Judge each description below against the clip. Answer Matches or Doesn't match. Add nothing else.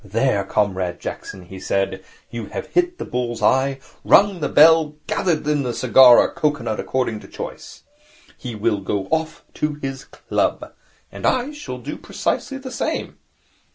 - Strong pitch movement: Matches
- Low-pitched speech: Matches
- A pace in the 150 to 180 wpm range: Matches